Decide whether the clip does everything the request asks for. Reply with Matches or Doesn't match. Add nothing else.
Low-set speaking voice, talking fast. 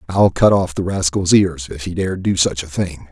Matches